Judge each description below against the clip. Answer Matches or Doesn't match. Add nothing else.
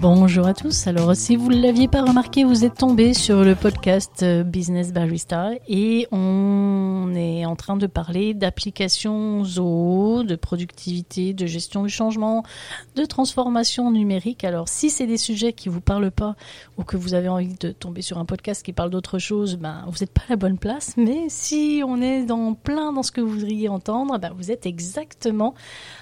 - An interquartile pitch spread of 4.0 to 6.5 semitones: Matches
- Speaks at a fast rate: Doesn't match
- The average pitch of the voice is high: Matches